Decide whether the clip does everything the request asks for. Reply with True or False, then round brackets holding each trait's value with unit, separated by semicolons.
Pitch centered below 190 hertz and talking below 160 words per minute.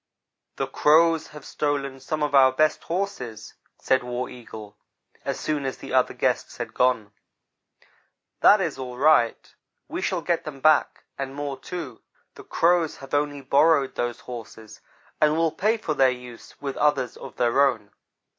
False (135 Hz; 165 wpm)